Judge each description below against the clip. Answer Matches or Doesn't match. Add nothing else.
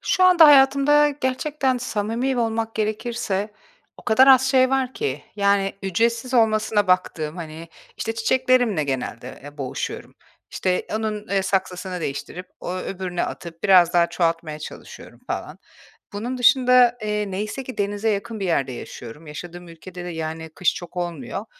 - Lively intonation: Matches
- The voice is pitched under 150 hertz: Doesn't match